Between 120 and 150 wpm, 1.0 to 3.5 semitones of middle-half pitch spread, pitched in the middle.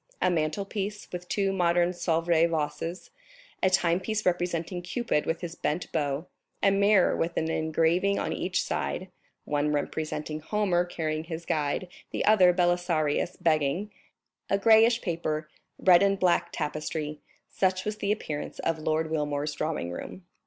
Yes: average, 140 wpm; average, 3.2 semitones; medium, 170 Hz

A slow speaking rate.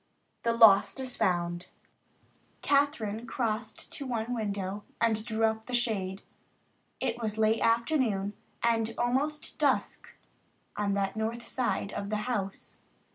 Yes: slow, 130 wpm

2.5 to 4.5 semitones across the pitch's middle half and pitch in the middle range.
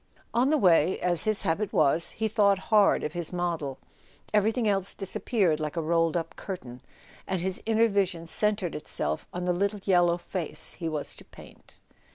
Yes: average, 3.7 semitones; medium, 180 Hz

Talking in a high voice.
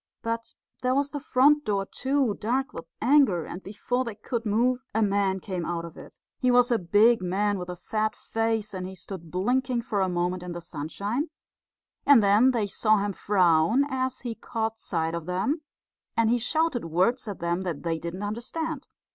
Yes: high, 215 Hz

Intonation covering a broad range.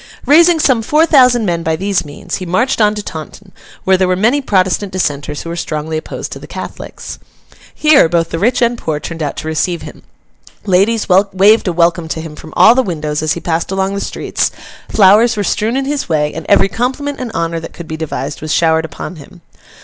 Yes: wide, 5.9 semitones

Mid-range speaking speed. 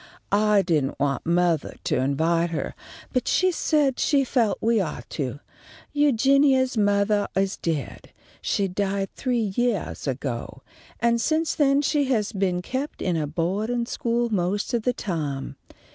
Yes: average, 145 wpm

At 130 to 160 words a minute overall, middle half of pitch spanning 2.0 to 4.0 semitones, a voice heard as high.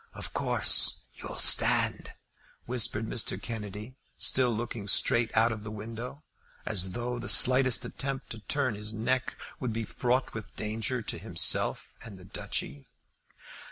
No: average, 145 wpm; average, 2.7 semitones; low, 115 Hz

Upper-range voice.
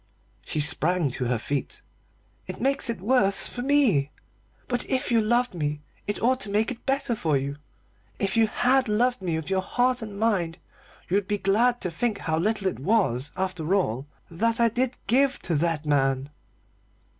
Yes: high, 200 Hz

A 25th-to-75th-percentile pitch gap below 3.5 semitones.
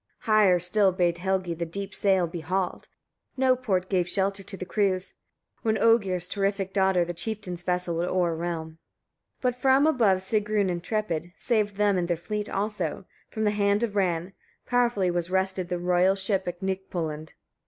Yes: average, 2.9 semitones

